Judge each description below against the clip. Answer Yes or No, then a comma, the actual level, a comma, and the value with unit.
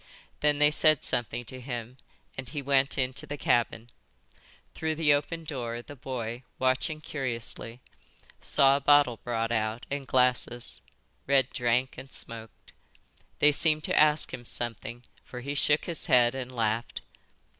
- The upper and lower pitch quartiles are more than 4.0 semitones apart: No, average, 3.4 semitones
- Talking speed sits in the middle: Yes, average, 150 wpm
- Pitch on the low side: Yes, low, 130 Hz